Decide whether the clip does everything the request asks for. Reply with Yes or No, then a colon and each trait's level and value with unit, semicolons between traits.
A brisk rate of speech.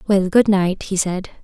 Yes: fast, 210 wpm